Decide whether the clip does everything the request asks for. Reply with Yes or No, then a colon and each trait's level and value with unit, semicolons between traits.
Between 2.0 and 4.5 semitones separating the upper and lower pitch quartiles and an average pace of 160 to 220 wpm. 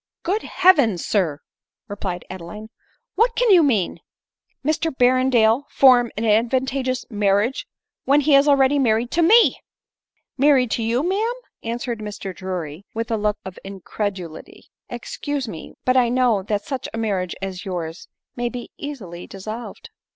No: wide, 5.4 semitones; average, 165 wpm